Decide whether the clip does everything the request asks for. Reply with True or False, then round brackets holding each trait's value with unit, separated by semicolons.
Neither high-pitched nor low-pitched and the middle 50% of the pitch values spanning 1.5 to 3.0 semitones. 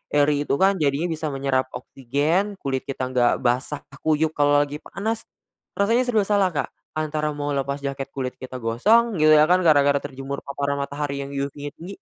True (145 Hz; 2.4 semitones)